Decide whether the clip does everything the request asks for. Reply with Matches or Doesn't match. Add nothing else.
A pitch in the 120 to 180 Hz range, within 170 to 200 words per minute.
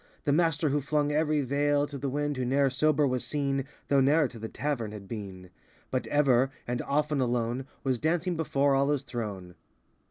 Matches